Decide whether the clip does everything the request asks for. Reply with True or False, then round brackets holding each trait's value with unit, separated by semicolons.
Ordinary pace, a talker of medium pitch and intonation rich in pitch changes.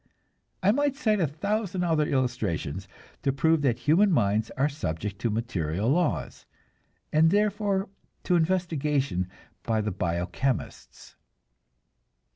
False (120 wpm; 145 Hz; 9.0 semitones)